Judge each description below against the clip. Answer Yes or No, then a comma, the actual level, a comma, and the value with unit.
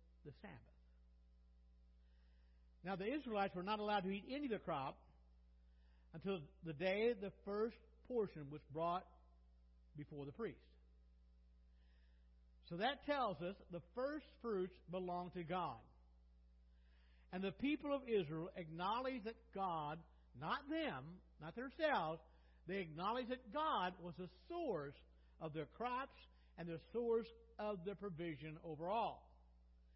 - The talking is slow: Yes, slow, 130 wpm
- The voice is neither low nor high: Yes, medium, 165 Hz